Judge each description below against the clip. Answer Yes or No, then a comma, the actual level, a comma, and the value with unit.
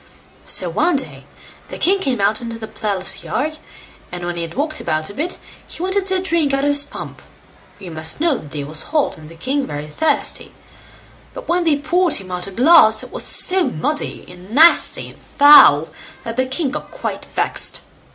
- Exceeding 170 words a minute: Yes, fast, 205 wpm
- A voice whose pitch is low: No, very high, 265 Hz